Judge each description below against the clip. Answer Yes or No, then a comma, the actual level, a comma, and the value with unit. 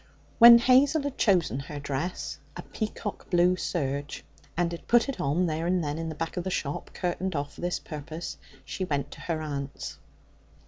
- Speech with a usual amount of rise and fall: Yes, average, 4.3 semitones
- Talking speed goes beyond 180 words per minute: Yes, average, 190 wpm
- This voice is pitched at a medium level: Yes, medium, 170 Hz